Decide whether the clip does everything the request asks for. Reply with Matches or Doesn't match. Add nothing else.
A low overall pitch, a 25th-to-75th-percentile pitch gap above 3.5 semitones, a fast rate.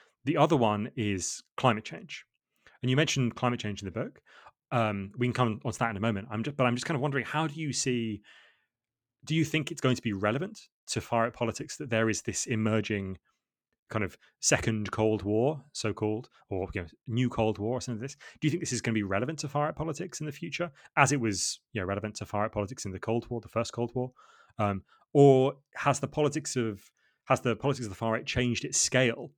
Matches